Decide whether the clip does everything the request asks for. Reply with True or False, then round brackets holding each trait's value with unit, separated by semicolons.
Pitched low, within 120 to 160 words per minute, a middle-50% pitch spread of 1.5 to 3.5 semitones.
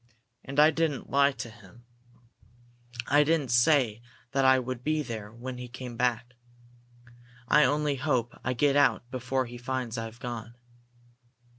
True (125 Hz; 150 wpm; 2.9 semitones)